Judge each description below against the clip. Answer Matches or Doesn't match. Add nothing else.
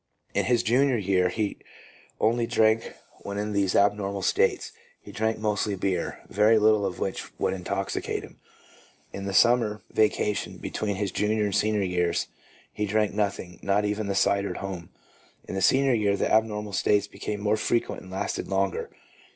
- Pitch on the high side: Doesn't match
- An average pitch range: Doesn't match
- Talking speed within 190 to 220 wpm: Doesn't match